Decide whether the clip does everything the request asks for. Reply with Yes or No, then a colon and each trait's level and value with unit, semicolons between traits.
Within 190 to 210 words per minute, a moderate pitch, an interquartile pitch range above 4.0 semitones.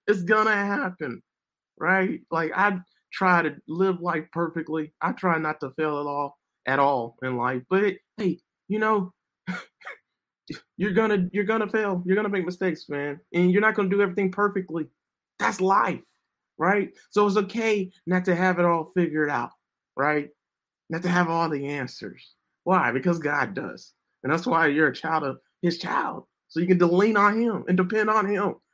No: average, 180 wpm; medium, 180 Hz; average, 4.6 semitones